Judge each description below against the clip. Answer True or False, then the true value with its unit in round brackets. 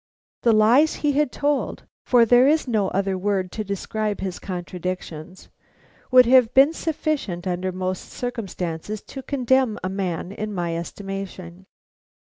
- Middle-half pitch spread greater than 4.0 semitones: True (5.4 semitones)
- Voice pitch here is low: False (200 Hz)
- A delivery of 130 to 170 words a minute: True (140 wpm)